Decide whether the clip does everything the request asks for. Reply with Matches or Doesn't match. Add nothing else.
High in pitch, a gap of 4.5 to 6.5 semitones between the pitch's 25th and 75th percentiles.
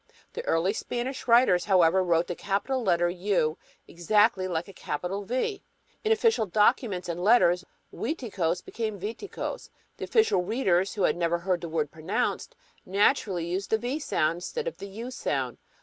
Matches